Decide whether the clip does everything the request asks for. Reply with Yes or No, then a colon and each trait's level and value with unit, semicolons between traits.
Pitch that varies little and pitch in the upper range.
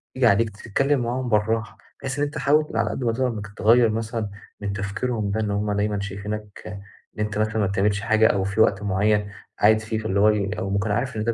No: narrow, 2.1 semitones; low, 105 Hz